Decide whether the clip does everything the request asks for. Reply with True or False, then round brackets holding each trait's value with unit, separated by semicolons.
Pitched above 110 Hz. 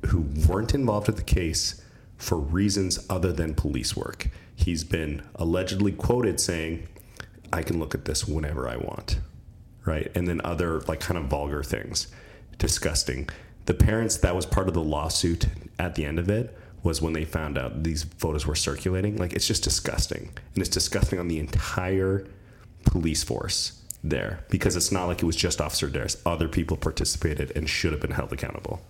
False (85 Hz)